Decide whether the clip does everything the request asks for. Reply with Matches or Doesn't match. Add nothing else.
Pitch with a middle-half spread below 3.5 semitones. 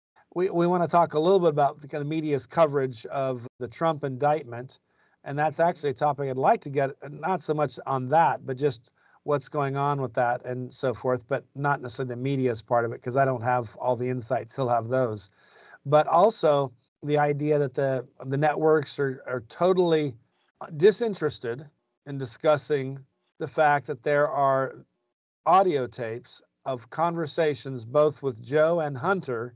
Matches